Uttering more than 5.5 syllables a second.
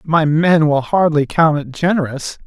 No: 4.8 syllables/s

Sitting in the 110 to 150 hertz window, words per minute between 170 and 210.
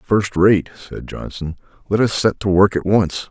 No: very low, 95 Hz; average, 200 wpm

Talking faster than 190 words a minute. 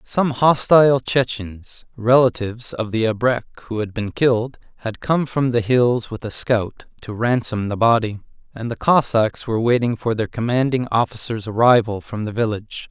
No: average, 165 wpm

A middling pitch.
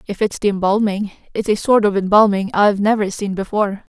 No: high, 205 Hz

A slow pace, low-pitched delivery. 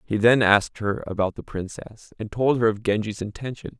No: fast, 205 wpm; low, 110 Hz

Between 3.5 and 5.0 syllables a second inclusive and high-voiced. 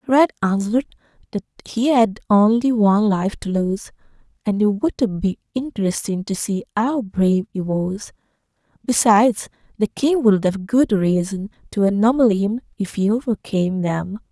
Yes: 4.6 syllables/s; high, 215 Hz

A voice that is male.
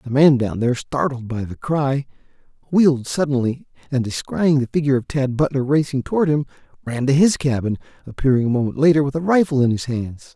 Yes: male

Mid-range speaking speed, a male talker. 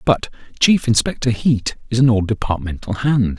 Yes: average, 160 wpm; male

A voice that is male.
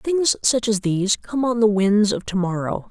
No: female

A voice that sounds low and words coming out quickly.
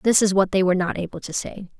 No: high, 190 Hz; fast, 300 wpm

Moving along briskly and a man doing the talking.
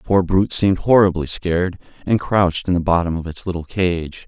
Yes: fast, 210 wpm; male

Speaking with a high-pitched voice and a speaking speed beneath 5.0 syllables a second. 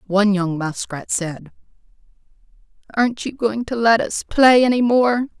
Yes: high, 195 Hz; 4.6 syllables/s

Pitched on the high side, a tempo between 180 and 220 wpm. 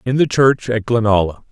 No: low, 115 Hz; average, 200 wpm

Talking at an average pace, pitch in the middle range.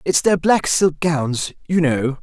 Yes: average, 190 wpm; medium, 160 Hz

